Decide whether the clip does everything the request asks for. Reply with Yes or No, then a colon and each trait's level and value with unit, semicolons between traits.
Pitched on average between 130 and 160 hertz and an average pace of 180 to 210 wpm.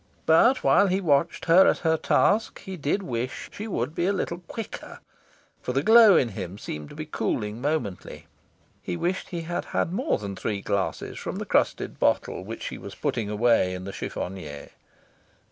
Yes: medium, 140 Hz; average, 185 wpm